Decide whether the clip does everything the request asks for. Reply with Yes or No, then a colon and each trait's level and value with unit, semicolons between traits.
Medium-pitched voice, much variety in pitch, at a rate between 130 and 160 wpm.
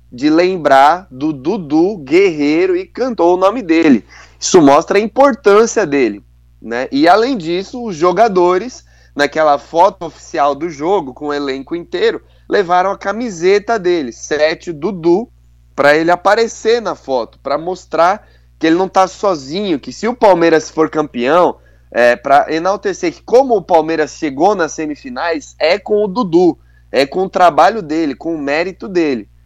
Yes: medium, 180 Hz; wide, 7.2 semitones; average, 155 wpm